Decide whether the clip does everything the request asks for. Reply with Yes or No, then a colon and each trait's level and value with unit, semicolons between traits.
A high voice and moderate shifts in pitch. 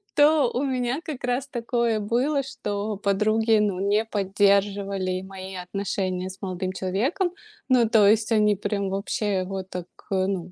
Yes: high, 205 Hz; average, 3.6 semitones